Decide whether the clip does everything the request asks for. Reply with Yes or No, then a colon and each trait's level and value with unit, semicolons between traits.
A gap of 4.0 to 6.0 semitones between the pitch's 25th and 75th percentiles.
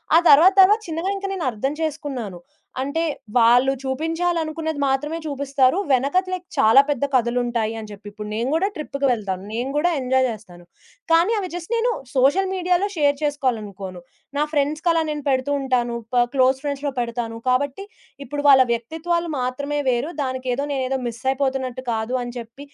Yes: average, 4.4 semitones